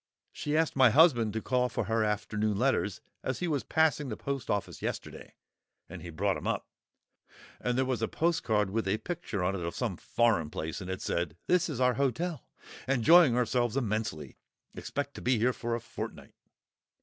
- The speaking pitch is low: Yes, low, 120 Hz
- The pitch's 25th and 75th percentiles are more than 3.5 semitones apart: Yes, average, 4.7 semitones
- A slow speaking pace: No, average, 185 wpm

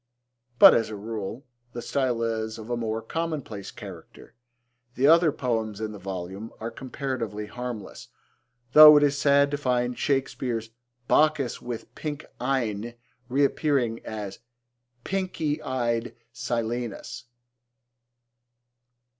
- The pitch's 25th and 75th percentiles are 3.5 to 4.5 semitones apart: Yes, average, 4.1 semitones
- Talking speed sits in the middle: No, slow, 115 wpm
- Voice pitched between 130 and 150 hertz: No, low, 120 Hz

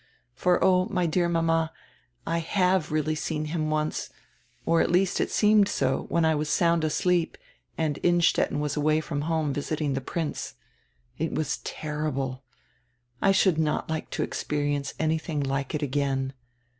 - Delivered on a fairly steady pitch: Yes, narrow, 2.3 semitones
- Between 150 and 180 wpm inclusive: Yes, average, 160 wpm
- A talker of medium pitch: Yes, medium, 155 Hz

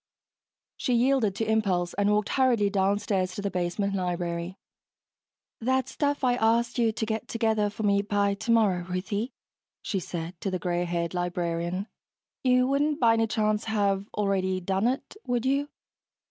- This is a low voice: No, high, 205 Hz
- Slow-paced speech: No, average, 160 wpm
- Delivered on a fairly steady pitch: No, average, 3.8 semitones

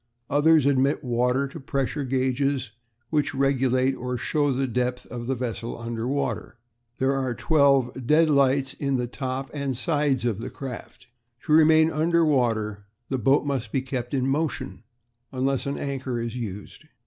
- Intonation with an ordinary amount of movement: No, narrow, 2.2 semitones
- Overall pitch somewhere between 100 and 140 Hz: Yes, low, 135 Hz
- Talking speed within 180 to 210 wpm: No, average, 160 wpm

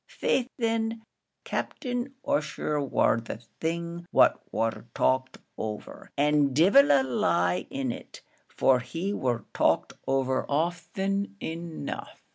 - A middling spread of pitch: No, wide, 7.1 semitones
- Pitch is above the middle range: No, medium, 150 Hz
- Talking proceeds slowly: Yes, slow, 115 wpm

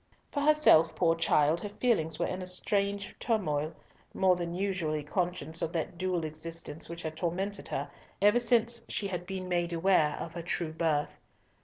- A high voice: No, medium, 175 Hz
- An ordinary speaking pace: Yes, average, 175 wpm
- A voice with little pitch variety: No, average, 3.5 semitones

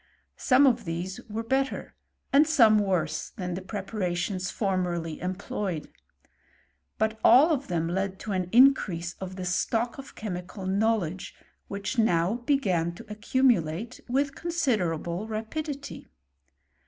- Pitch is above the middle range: Yes, high, 200 Hz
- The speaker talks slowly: Yes, slow, 110 wpm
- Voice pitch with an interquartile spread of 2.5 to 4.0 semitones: No, average, 5.1 semitones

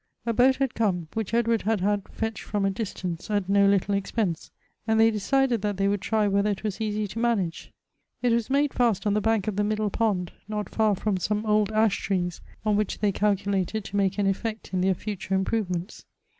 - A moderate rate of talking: No, fast, 215 wpm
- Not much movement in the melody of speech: Yes, narrow, 2.2 semitones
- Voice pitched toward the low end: No, high, 210 Hz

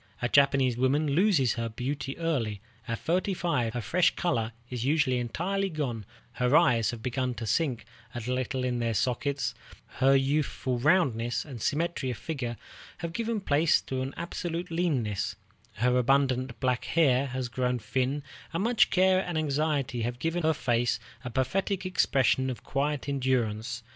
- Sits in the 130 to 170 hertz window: Yes, low, 135 Hz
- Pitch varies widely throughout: No, average, 4.7 semitones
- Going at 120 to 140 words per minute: No, average, 160 wpm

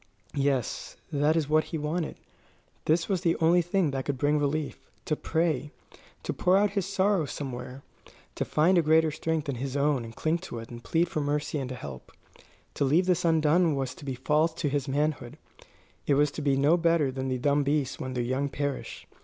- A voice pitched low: No, medium, 150 Hz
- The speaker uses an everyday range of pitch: Yes, average, 3.1 semitones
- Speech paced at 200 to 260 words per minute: Yes, fast, 205 wpm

